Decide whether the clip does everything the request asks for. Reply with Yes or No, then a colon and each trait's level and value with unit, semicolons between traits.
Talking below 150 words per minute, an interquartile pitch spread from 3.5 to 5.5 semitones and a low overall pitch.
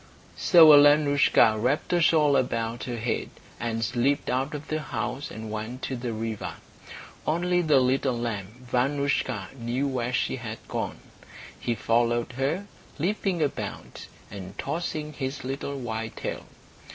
Yes: average, 140 wpm; average, 3.9 semitones; low, 130 Hz